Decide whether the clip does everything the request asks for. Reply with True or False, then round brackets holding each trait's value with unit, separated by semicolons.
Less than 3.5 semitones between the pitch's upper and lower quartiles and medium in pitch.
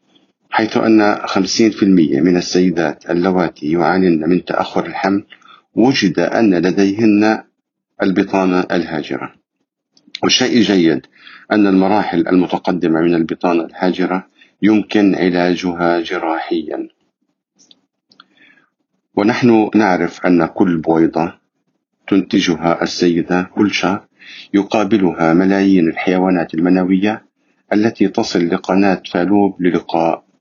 False (2.9 semitones; 90 Hz)